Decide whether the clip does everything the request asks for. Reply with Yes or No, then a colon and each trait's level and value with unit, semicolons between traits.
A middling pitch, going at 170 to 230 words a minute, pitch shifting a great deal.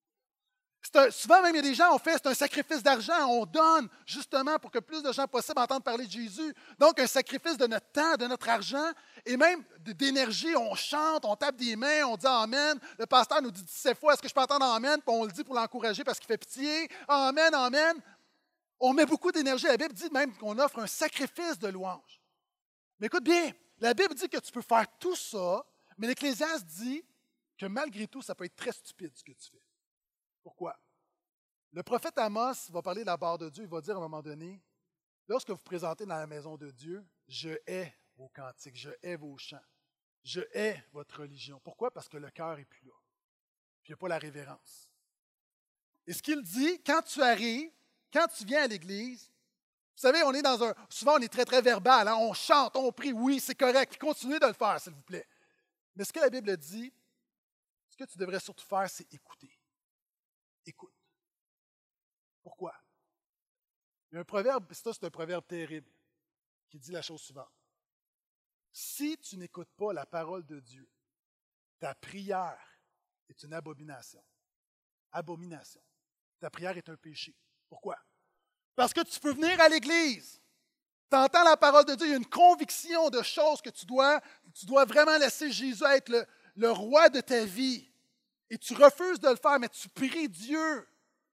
No: very high, 250 Hz; average, 200 wpm; wide, 8.1 semitones